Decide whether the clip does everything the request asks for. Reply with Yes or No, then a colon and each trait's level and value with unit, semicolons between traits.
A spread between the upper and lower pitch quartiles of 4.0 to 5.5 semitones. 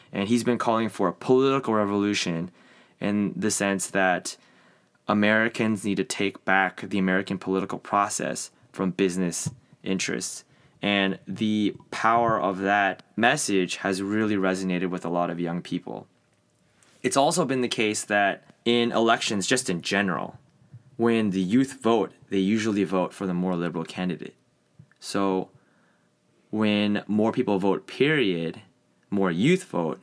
No: average, 3.2 semitones